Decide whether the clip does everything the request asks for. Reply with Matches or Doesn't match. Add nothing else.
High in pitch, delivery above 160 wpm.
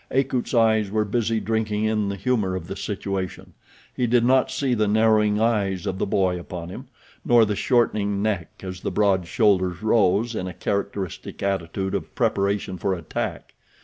Doesn't match